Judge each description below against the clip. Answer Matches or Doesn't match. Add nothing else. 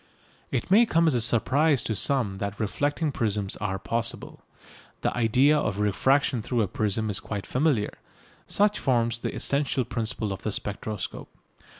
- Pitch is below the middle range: Matches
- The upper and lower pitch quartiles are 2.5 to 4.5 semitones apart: Doesn't match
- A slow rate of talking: Doesn't match